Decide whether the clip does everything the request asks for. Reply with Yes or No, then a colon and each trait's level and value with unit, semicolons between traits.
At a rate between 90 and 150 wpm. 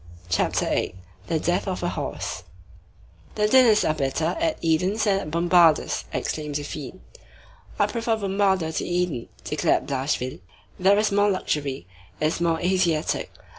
Yes: average, 140 wpm